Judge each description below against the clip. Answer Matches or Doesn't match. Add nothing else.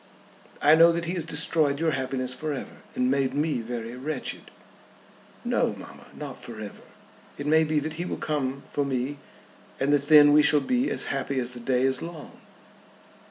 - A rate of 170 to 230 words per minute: Matches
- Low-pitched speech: Doesn't match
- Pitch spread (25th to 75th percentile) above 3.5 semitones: Doesn't match